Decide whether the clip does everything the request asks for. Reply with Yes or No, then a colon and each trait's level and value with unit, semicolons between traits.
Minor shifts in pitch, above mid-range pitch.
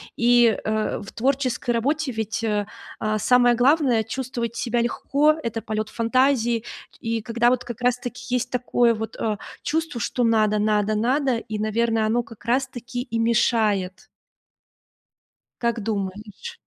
Yes: narrow, 2.3 semitones; high, 235 Hz